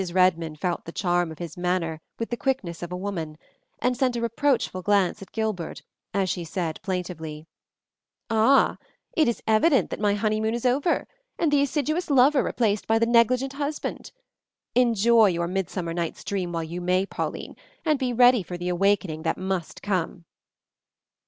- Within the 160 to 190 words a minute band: Yes, average, 170 wpm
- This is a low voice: No, high, 200 Hz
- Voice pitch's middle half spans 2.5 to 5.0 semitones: No, wide, 5.5 semitones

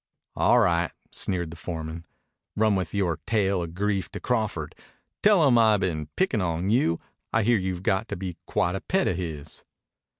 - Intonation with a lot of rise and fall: No, average, 4.3 semitones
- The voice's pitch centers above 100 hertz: No, very low, 95 Hz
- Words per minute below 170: No, average, 180 wpm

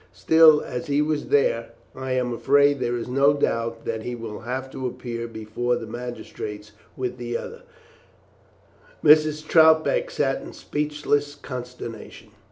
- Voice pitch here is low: Yes, low, 130 Hz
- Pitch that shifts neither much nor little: Yes, average, 3.9 semitones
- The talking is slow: No, average, 145 wpm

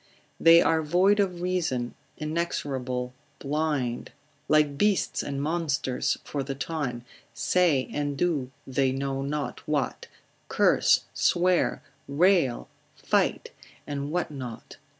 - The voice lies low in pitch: No, medium, 145 Hz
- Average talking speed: No, slow, 110 wpm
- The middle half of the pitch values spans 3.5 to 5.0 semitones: Yes, average, 4.0 semitones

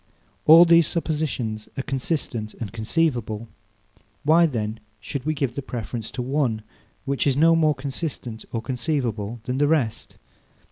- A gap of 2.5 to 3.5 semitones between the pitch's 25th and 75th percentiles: No, average, 5.2 semitones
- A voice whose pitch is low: Yes, low, 130 Hz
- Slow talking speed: No, average, 145 wpm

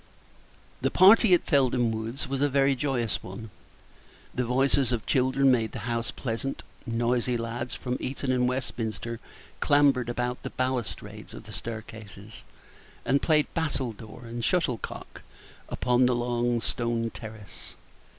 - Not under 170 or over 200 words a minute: No, slow, 135 wpm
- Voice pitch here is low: Yes, low, 125 Hz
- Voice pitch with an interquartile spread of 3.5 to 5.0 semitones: No, narrow, 2.5 semitones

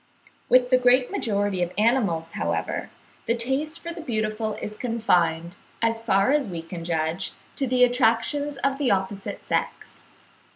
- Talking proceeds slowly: No, average, 155 wpm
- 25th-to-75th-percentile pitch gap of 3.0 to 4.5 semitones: No, wide, 5.5 semitones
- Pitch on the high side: Yes, high, 225 Hz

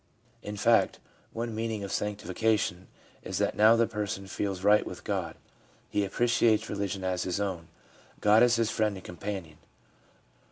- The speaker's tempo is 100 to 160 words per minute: Yes, average, 155 wpm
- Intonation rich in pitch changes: No, narrow, 2.6 semitones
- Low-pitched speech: Yes, low, 105 Hz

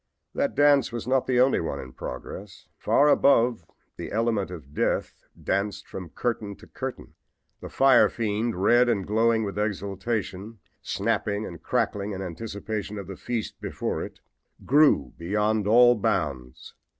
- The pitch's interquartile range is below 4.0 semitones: Yes, average, 3.5 semitones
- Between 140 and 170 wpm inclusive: Yes, average, 150 wpm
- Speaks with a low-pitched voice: Yes, low, 105 Hz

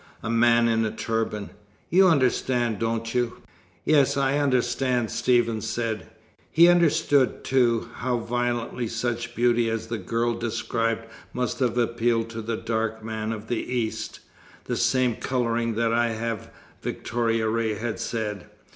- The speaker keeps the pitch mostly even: Yes, narrow, 1.5 semitones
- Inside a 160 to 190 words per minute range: No, average, 145 wpm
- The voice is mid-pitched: No, low, 115 Hz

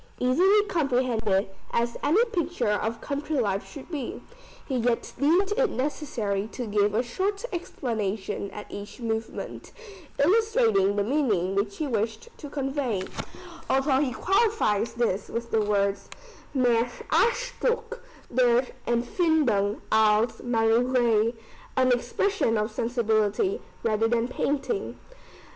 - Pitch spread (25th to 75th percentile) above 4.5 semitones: Yes, wide, 5.6 semitones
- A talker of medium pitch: No, high, 240 Hz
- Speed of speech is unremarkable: No, slow, 120 wpm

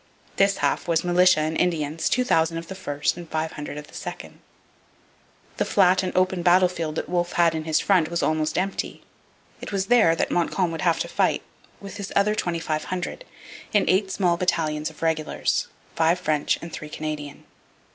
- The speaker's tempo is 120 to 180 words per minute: Yes, average, 175 wpm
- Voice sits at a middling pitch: Yes, medium, 170 Hz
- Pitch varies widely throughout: No, average, 2.8 semitones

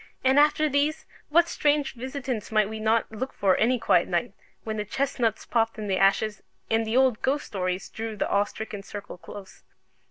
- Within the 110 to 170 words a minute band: No, average, 190 wpm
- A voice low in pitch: No, high, 225 Hz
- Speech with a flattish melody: No, average, 4.1 semitones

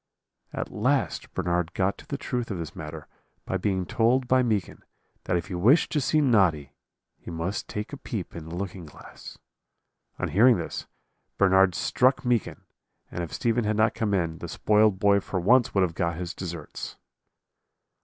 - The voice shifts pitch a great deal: No, average, 4.9 semitones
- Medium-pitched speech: No, very low, 95 Hz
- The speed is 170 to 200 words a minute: Yes, average, 180 wpm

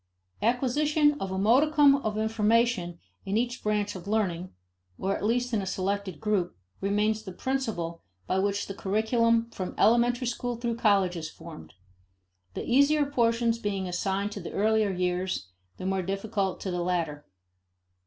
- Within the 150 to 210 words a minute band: Yes, average, 155 wpm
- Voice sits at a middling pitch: No, high, 210 Hz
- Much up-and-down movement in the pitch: No, average, 3.8 semitones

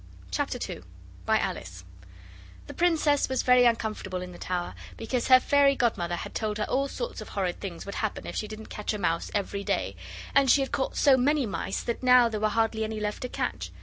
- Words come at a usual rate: No, fast, 215 wpm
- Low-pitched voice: No, high, 220 Hz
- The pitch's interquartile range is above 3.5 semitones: Yes, average, 4.6 semitones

